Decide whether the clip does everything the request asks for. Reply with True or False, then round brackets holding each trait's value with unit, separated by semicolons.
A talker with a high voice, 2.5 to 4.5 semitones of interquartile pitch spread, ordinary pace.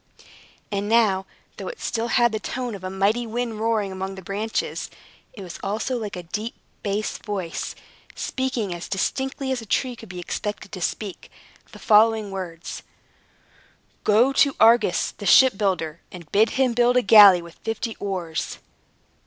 True (210 Hz; 3.5 semitones; 160 wpm)